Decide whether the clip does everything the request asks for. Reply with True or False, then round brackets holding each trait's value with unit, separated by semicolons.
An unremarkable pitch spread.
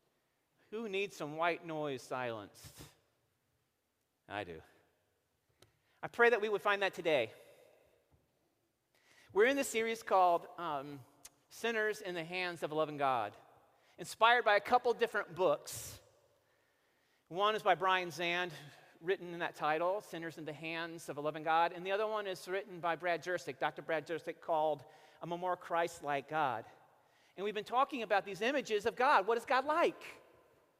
False (5.8 semitones)